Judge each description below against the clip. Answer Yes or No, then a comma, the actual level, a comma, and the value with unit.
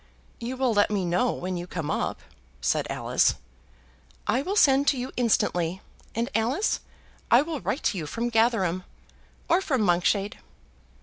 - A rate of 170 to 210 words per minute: No, average, 160 wpm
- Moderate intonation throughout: No, wide, 6.1 semitones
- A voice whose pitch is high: Yes, high, 225 Hz